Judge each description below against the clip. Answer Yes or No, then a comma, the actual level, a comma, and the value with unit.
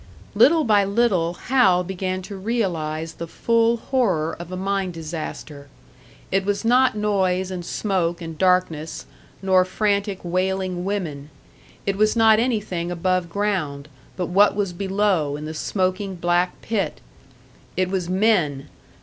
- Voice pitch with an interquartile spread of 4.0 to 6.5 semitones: No, average, 3.0 semitones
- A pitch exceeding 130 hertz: Yes, medium, 185 Hz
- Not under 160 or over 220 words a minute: No, average, 140 wpm